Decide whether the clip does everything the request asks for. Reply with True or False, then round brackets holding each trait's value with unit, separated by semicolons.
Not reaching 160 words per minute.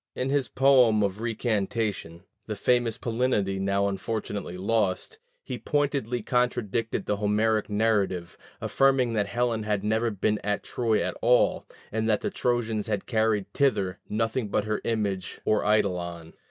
True (145 wpm)